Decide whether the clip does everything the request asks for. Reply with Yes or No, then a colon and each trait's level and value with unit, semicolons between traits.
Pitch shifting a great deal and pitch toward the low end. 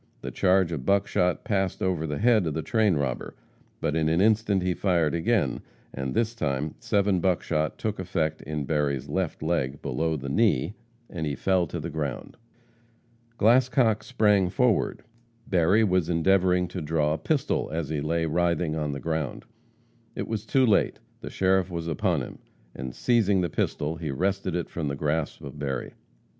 No: average, 4.5 semitones; very low, 85 Hz